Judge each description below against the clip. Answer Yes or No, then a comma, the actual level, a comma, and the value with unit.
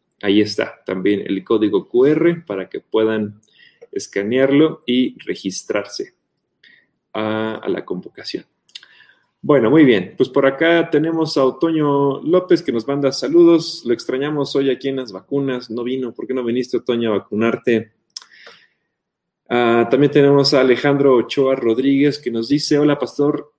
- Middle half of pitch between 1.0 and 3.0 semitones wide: No, average, 4.2 semitones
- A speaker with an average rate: Yes, average, 150 wpm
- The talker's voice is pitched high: No, low, 135 Hz